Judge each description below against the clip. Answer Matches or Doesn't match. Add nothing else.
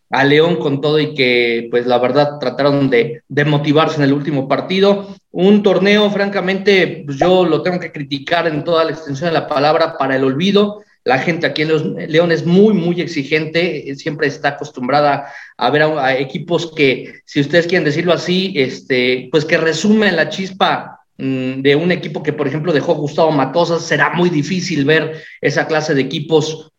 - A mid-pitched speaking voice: Matches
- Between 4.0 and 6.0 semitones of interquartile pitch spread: Doesn't match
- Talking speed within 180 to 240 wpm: Matches